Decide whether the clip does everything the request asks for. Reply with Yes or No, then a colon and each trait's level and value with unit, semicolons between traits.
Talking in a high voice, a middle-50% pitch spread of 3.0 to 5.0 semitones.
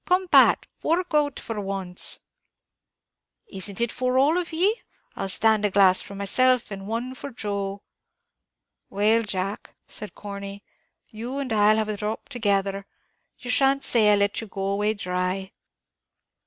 Yes: high, 210 Hz; average, 4.2 semitones